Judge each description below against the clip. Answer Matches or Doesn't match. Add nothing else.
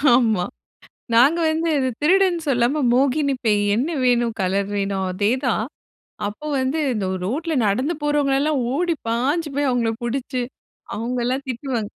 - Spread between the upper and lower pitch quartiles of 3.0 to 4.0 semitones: Doesn't match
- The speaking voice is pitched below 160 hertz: Doesn't match